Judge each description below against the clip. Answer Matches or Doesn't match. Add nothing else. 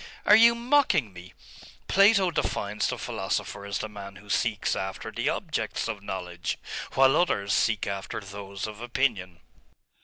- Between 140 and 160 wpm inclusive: Matches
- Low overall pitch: Matches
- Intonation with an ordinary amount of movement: Doesn't match